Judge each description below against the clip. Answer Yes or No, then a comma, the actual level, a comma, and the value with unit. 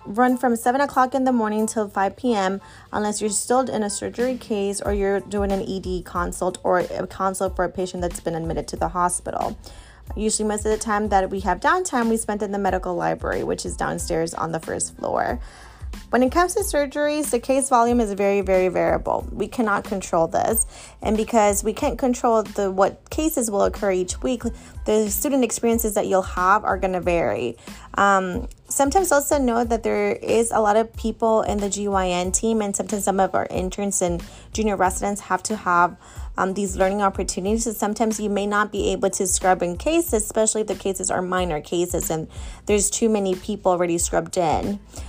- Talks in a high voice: Yes, high, 205 Hz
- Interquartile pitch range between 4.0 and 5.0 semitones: No, average, 3.3 semitones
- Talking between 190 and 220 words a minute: Yes, fast, 205 wpm